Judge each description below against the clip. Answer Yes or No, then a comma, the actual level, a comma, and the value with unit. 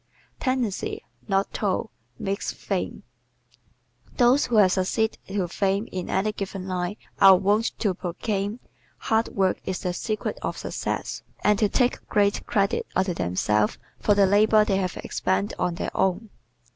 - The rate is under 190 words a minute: Yes, average, 155 wpm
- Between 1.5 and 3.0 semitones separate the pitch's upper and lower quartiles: Yes, narrow, 2.4 semitones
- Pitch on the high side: Yes, high, 195 Hz